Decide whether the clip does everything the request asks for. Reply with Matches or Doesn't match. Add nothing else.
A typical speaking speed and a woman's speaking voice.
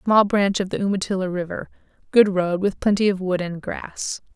Matches